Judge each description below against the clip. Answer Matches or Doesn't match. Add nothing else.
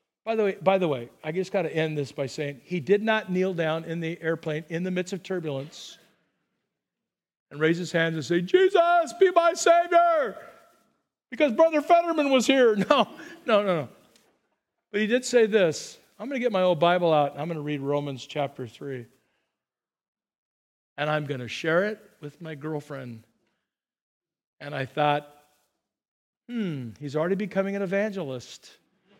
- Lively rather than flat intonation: Matches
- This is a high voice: Doesn't match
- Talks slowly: Doesn't match